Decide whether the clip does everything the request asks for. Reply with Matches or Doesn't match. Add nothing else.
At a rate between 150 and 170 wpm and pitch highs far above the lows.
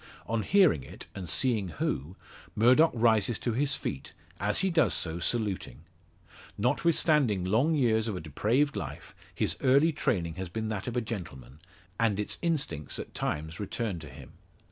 Matches